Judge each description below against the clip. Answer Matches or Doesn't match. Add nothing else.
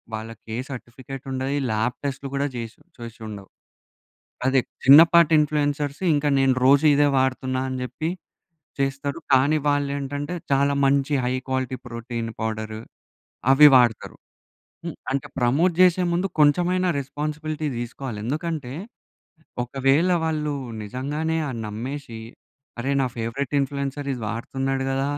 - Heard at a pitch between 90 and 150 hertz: Matches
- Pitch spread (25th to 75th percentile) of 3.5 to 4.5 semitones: Doesn't match